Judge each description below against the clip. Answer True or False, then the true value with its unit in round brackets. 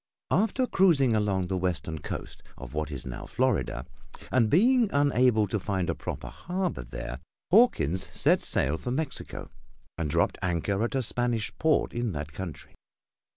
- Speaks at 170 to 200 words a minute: False (155 wpm)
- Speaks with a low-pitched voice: True (105 Hz)